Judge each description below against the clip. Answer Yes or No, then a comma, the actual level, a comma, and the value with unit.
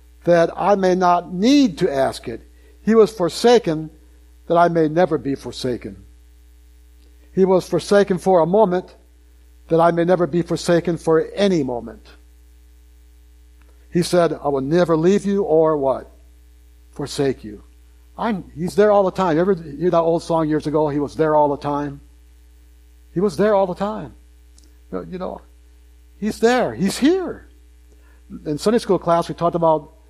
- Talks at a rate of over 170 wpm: No, average, 165 wpm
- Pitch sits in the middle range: Yes, medium, 150 Hz